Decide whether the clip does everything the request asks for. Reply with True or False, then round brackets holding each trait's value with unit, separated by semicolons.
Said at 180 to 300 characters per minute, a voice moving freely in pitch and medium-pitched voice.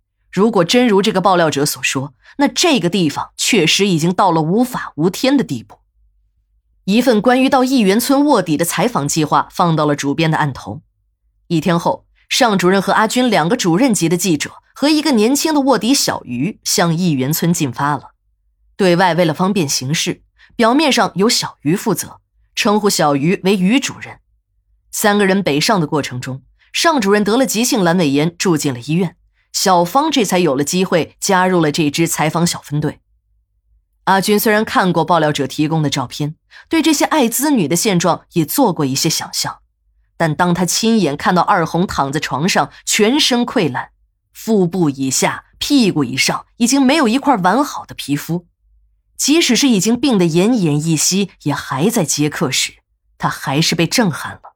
True (265 characters per minute; 6.7 semitones; 180 Hz)